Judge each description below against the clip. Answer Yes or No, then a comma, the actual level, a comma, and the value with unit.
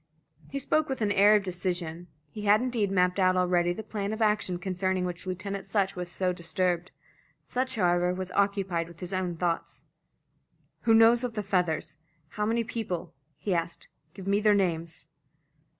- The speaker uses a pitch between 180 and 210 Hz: Yes, high, 190 Hz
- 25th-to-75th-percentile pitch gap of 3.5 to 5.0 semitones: No, average, 3.0 semitones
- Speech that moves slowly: No, average, 175 wpm